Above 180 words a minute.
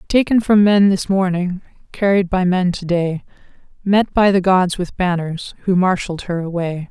No: average, 175 wpm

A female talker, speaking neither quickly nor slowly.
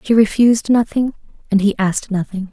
Yes: female; average, 165 wpm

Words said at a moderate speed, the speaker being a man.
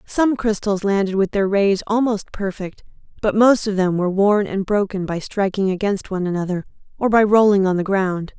No: average, 195 wpm; female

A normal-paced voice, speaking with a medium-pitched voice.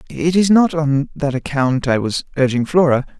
Yes: average, 190 wpm; medium, 145 Hz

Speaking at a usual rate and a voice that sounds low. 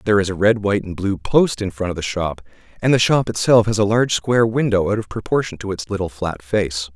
No: fast, 260 wpm; low, 100 Hz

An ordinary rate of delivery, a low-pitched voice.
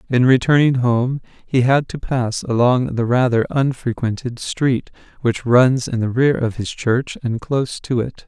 Yes: average, 175 wpm; low, 125 Hz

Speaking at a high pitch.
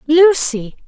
Yes: very high, 295 Hz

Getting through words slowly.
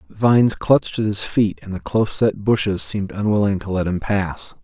No: fast, 205 wpm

